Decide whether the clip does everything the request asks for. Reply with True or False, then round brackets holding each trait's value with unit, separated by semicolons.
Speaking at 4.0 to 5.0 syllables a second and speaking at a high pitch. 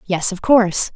True (4.7 syllables/s; 200 Hz)